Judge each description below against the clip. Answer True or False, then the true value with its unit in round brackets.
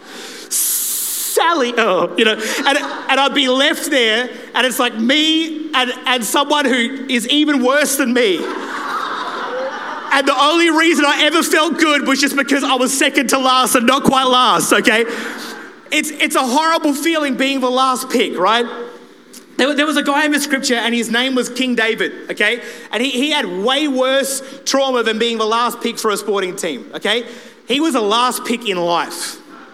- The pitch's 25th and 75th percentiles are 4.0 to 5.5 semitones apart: False (3.4 semitones)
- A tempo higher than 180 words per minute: True (190 wpm)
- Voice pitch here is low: False (260 Hz)